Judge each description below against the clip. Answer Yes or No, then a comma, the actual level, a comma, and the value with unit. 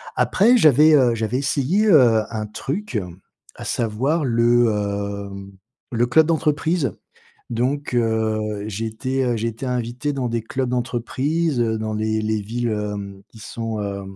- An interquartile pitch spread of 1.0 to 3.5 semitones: No, average, 3.9 semitones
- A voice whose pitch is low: Yes, low, 120 Hz